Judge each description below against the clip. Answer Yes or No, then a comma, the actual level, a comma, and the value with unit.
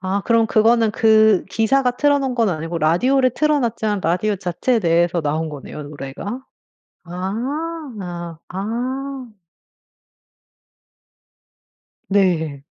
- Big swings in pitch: Yes, wide, 6.5 semitones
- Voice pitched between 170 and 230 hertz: Yes, high, 210 Hz